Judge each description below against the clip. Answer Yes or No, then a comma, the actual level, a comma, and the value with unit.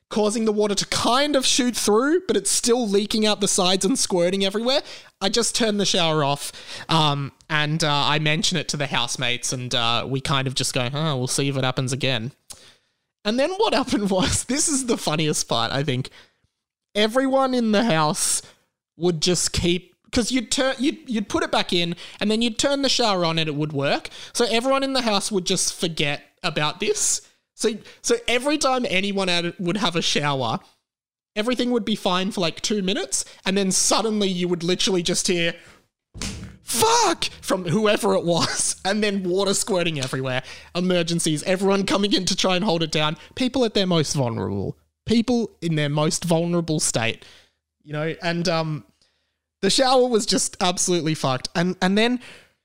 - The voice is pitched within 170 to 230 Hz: Yes, medium, 185 Hz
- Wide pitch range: Yes, wide, 6.4 semitones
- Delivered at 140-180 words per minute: No, average, 190 wpm